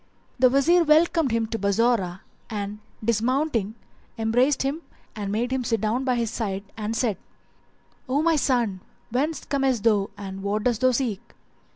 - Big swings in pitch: No, average, 4.1 semitones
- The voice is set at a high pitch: Yes, high, 235 Hz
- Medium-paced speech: Yes, average, 160 wpm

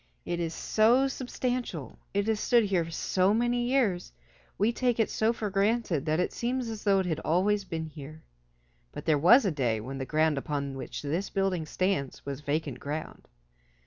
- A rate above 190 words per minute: No, average, 185 wpm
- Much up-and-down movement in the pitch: Yes, wide, 6.3 semitones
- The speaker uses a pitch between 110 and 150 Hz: No, medium, 185 Hz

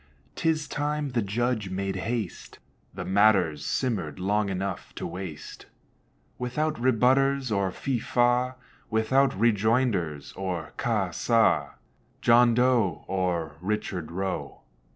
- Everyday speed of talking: No, slow, 110 wpm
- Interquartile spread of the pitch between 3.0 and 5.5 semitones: Yes, average, 4.9 semitones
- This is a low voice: Yes, low, 110 Hz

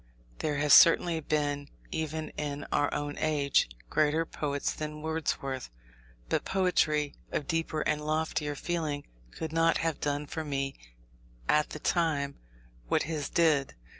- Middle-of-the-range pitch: Yes, medium, 150 Hz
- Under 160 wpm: Yes, slow, 135 wpm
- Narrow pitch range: Yes, narrow, 1.8 semitones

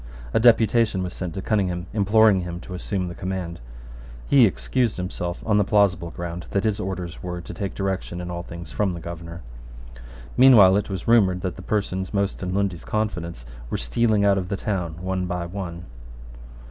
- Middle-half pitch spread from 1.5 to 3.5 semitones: Yes, average, 2.7 semitones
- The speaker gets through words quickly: No, average, 185 wpm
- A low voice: Yes, very low, 95 Hz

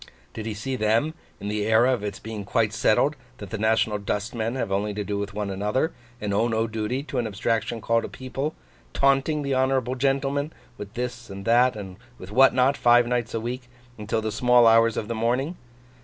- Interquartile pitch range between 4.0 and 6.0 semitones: No, average, 3.3 semitones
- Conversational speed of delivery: No, fast, 215 wpm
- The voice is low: Yes, low, 115 Hz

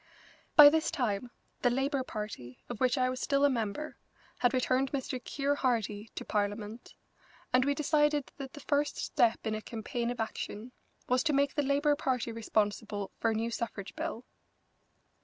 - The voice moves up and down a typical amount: Yes, average, 4.3 semitones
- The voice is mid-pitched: No, very high, 250 Hz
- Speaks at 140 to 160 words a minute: No, average, 175 wpm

